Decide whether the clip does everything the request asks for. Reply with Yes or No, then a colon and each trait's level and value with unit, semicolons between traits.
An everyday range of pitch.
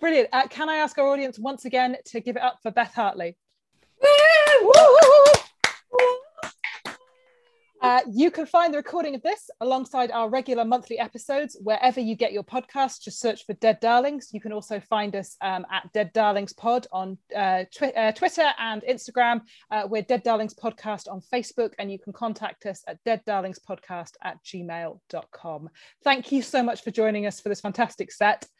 Yes: average, 4.5 semitones